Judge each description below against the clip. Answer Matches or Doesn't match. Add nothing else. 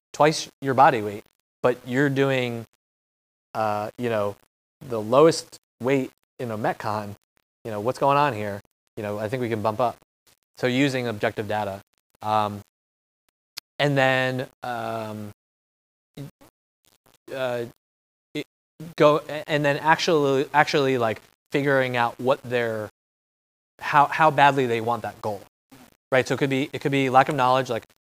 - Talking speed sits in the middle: Matches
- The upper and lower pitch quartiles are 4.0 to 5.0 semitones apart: Matches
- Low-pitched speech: Matches